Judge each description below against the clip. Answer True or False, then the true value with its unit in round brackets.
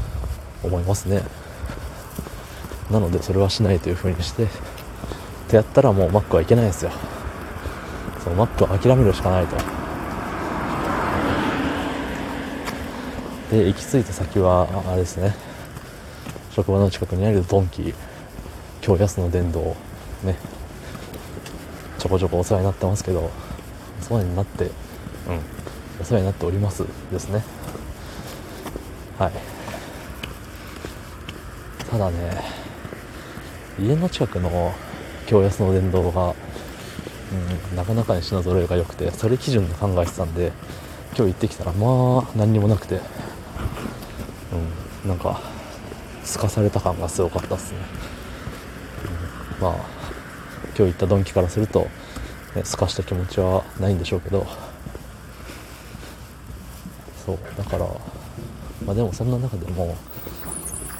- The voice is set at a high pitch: False (95 Hz)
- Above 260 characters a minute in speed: False (250 characters per minute)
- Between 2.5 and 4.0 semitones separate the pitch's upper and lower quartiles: True (2.9 semitones)